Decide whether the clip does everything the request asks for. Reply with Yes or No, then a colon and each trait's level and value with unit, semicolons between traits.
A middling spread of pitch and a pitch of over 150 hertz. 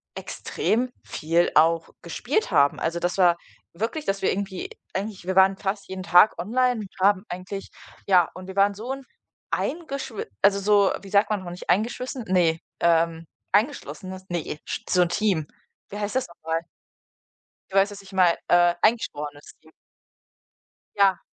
Yes: average, 3.2 semitones; high, 190 Hz